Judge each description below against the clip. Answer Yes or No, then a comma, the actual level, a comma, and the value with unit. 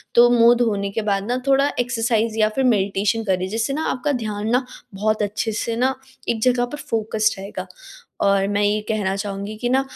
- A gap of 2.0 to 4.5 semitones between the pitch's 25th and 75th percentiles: Yes, average, 3.0 semitones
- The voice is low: No, high, 220 Hz